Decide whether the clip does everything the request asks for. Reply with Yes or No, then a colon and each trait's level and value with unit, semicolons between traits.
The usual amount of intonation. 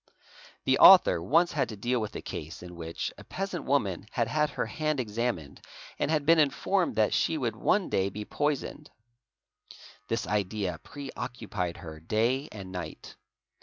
No: wide, 7.4 semitones